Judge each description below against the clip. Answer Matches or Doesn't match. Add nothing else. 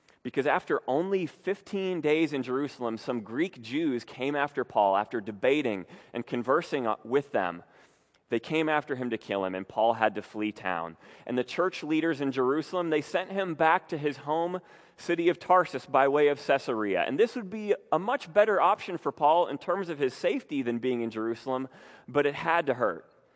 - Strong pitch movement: Matches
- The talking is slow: Doesn't match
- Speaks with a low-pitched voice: Doesn't match